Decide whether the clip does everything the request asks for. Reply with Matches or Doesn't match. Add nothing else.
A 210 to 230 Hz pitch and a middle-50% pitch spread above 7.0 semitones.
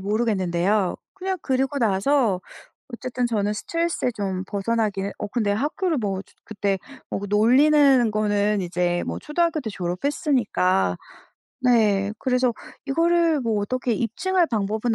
Doesn't match